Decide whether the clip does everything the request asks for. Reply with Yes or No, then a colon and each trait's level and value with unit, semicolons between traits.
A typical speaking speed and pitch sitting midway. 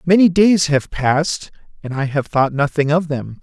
Yes: average, 195 wpm; medium, 150 Hz